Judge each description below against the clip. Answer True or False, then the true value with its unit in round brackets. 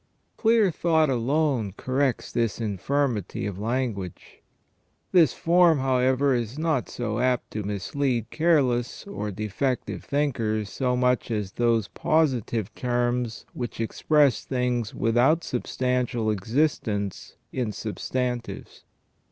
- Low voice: True (125 Hz)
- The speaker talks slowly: True (110 wpm)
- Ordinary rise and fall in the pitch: True (4.0 semitones)